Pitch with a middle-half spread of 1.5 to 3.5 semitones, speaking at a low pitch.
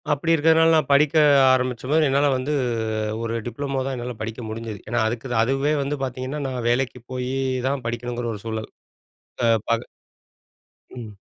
Yes: average, 3.0 semitones; low, 130 Hz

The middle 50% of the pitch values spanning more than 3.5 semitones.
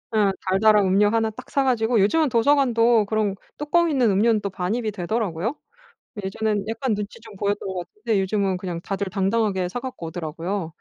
No: average, 3.1 semitones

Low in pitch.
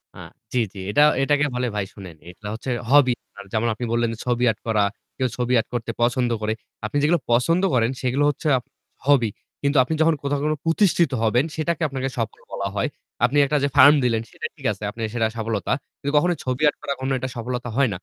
Yes: low, 125 Hz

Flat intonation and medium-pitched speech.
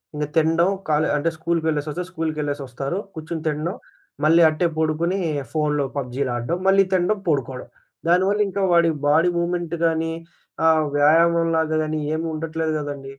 Yes: narrow, 2.2 semitones; medium, 160 Hz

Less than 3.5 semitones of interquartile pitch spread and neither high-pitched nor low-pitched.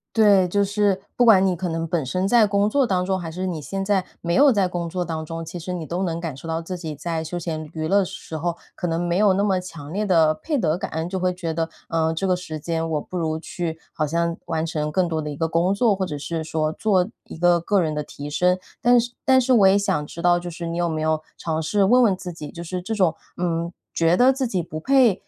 Yes: average, 3.0 semitones; medium, 175 Hz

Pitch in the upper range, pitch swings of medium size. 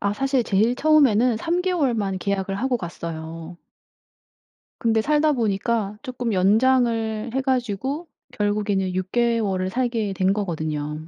Yes: high, 220 Hz; average, 4.6 semitones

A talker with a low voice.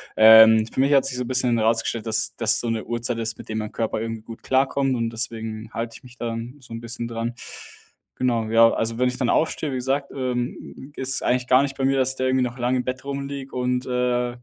Yes: low, 120 Hz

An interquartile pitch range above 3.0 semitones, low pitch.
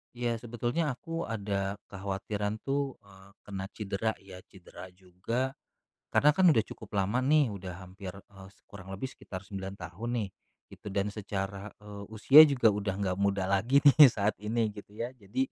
Yes: average, 3.7 semitones; low, 105 Hz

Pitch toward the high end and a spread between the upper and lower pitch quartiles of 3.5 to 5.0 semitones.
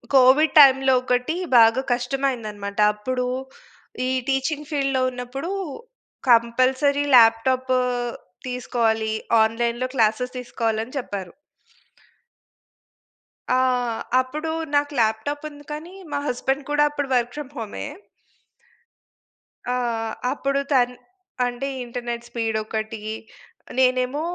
No: very high, 250 Hz; average, 3.1 semitones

